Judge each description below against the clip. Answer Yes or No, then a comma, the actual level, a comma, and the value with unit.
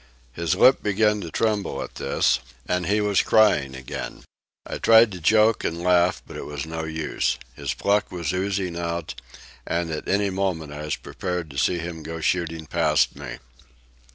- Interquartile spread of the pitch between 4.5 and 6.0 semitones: No, average, 3.8 semitones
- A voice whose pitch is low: Yes, very low, 85 Hz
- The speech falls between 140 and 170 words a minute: No, average, 180 wpm